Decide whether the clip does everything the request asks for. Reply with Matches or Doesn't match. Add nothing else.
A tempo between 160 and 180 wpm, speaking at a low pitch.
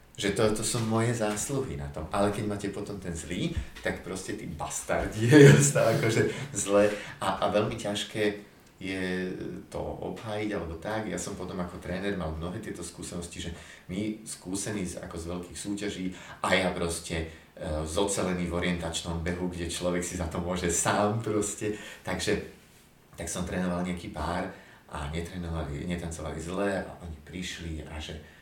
Matches